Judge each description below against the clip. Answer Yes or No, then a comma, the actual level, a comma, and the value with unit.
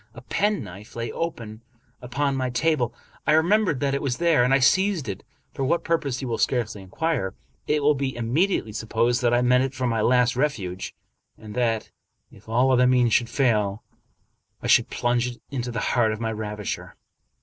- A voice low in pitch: Yes, low, 125 Hz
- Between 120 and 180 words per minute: No, average, 190 wpm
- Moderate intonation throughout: Yes, average, 3.6 semitones